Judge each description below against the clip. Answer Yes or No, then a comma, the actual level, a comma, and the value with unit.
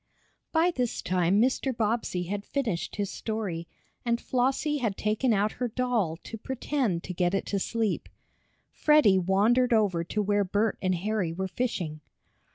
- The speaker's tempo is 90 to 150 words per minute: No, average, 160 wpm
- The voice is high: Yes, high, 210 Hz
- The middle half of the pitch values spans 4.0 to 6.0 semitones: Yes, average, 4.6 semitones